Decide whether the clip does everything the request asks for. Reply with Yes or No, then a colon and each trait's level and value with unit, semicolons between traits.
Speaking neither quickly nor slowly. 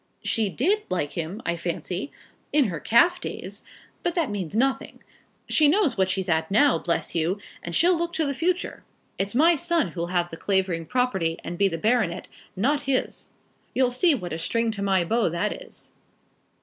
Yes: average, 190 wpm